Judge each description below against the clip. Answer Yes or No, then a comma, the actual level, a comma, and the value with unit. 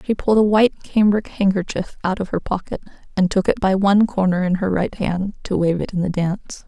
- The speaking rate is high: Yes, fast, 235 wpm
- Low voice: No, high, 190 Hz